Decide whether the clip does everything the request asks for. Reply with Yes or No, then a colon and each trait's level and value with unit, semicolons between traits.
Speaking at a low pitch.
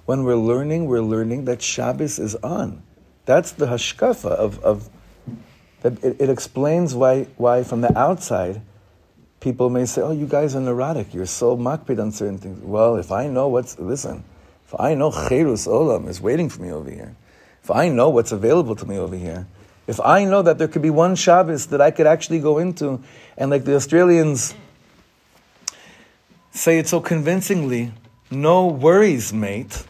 Yes: low, 130 Hz